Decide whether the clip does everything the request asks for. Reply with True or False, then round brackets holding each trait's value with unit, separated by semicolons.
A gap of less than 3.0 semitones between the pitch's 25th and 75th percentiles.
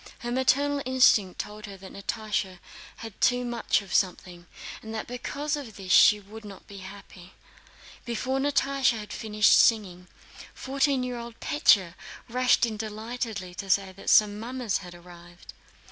False (4.3 semitones)